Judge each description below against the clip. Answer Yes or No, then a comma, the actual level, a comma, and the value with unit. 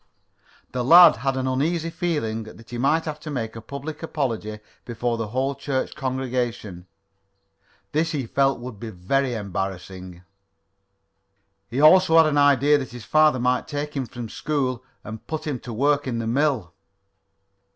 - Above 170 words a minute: No, average, 160 wpm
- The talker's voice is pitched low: Yes, low, 130 Hz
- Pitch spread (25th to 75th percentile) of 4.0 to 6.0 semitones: Yes, average, 4.4 semitones